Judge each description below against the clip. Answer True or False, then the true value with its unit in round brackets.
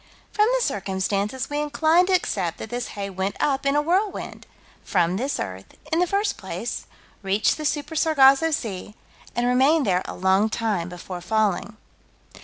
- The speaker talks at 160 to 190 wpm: True (170 wpm)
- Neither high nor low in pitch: False (240 Hz)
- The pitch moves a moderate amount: False (7.7 semitones)